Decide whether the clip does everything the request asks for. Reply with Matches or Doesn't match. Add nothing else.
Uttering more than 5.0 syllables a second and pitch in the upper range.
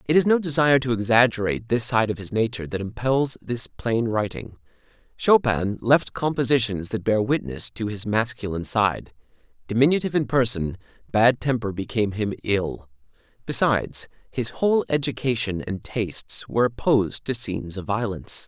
Doesn't match